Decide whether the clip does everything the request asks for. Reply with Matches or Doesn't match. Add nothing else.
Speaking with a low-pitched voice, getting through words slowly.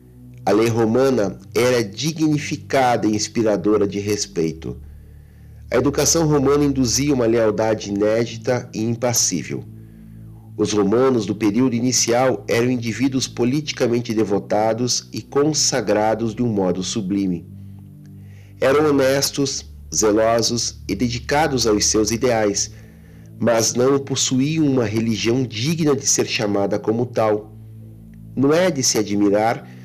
Matches